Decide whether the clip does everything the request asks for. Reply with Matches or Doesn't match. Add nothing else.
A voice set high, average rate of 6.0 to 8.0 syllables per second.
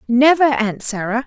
Doesn't match